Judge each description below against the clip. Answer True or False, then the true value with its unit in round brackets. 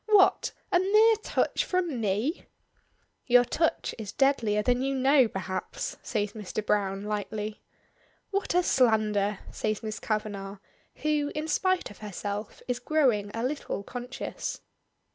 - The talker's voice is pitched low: False (230 Hz)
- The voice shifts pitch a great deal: True (6.3 semitones)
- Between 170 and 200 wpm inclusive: False (135 wpm)